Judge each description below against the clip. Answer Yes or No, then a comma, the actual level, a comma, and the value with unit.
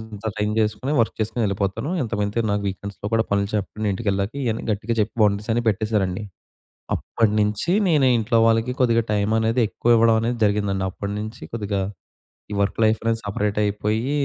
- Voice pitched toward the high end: No, low, 105 Hz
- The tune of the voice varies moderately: No, narrow, 2.0 semitones